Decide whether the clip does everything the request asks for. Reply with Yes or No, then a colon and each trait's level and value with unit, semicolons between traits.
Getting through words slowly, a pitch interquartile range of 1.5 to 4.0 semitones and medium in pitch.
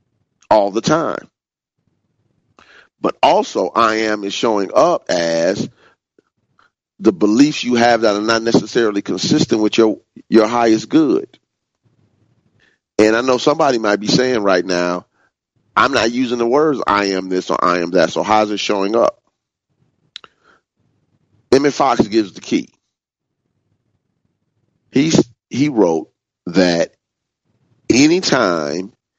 No: slow, 125 wpm; average, 3.3 semitones; low, 115 Hz